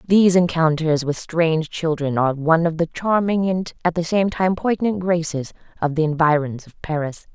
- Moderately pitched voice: Yes, medium, 165 Hz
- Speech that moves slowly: No, average, 180 wpm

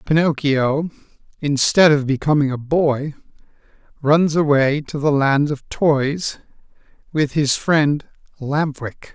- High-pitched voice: No, medium, 145 Hz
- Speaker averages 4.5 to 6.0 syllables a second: No, 3.7 syllables/s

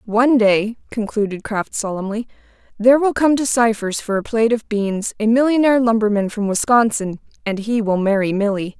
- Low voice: No, high, 220 Hz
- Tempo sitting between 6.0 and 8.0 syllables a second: No, 5.4 syllables/s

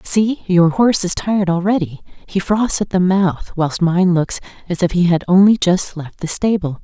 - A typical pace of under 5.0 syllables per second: Yes, 4.7 syllables/s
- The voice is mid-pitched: Yes, medium, 180 Hz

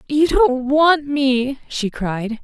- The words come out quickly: No, average, 150 wpm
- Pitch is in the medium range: No, very high, 270 Hz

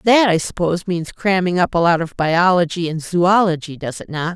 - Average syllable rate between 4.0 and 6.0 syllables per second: Yes, 5.2 syllables/s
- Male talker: No, female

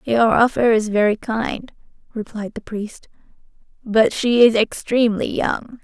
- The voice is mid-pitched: No, high, 225 Hz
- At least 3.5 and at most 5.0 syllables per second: Yes, 4.1 syllables/s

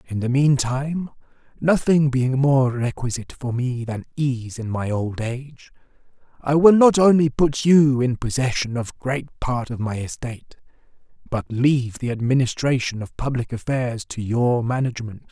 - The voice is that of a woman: No, male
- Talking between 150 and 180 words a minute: Yes, average, 155 wpm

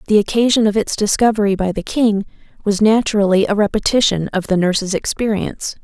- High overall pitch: Yes, high, 205 Hz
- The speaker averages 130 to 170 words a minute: Yes, average, 165 wpm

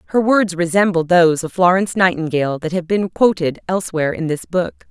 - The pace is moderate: Yes, average, 185 wpm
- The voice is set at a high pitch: No, medium, 175 Hz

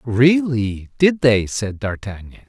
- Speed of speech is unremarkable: No, slow, 120 wpm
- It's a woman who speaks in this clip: No, male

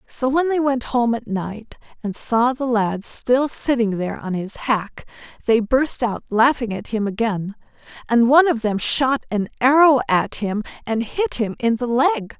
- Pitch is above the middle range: Yes, high, 240 Hz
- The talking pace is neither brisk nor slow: Yes, average, 190 wpm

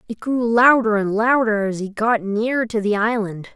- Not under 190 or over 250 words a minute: Yes, average, 200 wpm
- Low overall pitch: No, high, 220 Hz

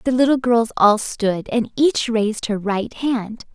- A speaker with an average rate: Yes, average, 185 wpm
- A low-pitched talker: No, high, 230 Hz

